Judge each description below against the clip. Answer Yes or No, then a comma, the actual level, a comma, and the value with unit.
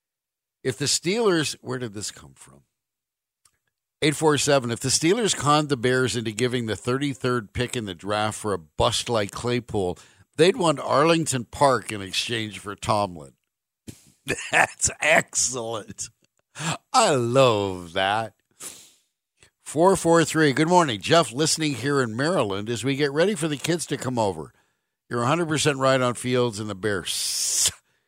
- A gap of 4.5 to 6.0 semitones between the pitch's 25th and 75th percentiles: Yes, average, 5.2 semitones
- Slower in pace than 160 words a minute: Yes, average, 145 wpm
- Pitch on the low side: Yes, low, 125 Hz